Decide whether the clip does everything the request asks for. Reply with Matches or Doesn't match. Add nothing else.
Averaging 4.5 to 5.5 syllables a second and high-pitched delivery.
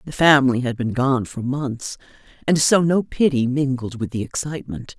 Doesn't match